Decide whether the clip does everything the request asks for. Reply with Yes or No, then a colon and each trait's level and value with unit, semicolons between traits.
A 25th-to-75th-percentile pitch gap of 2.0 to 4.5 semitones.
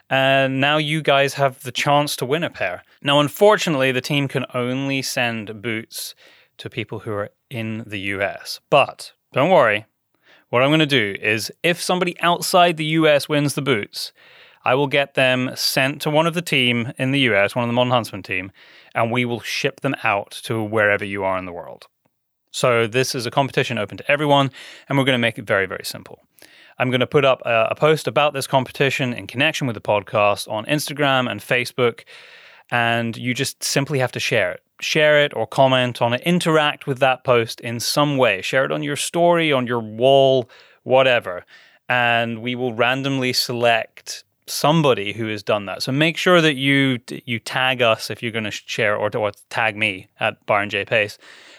Yes: average, 3.8 semitones